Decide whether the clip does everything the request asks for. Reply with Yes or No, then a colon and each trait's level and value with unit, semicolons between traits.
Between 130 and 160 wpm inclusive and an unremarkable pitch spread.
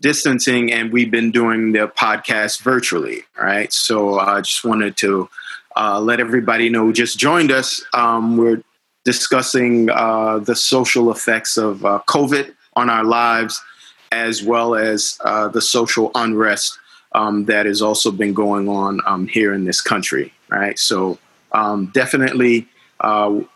No: average, 150 wpm; narrow, 2.2 semitones